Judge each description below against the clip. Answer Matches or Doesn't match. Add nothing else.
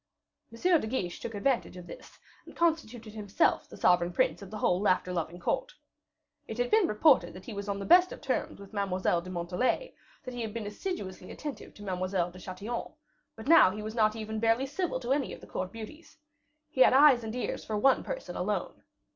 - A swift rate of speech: Matches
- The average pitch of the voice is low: Doesn't match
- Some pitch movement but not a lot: Doesn't match